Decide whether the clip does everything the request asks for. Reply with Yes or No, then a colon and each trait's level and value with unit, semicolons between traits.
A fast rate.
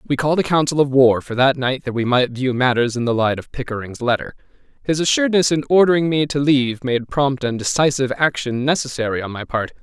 Yes: fast, 220 wpm